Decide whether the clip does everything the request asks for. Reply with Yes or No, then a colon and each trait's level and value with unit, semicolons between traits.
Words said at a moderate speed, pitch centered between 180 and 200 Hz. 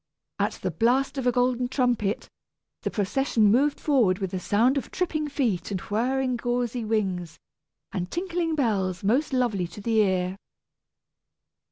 No: average, 150 wpm; high, 235 Hz